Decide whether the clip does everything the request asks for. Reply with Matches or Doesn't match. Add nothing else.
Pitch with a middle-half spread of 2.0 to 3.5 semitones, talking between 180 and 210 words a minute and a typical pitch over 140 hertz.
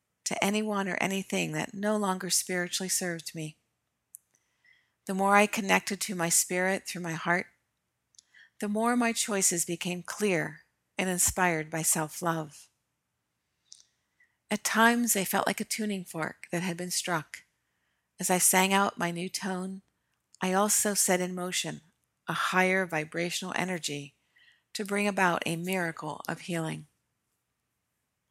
Doesn't match